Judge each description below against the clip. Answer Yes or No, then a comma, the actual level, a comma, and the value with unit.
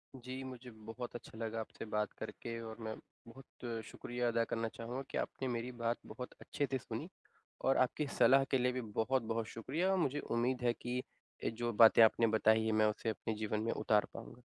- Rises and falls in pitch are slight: Yes, narrow, 2.1 semitones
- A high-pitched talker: No, low, 115 Hz